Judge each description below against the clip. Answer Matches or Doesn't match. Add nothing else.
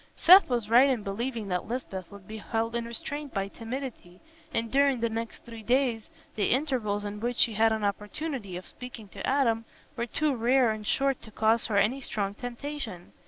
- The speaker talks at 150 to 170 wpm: Doesn't match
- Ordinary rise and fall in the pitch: Matches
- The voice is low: Doesn't match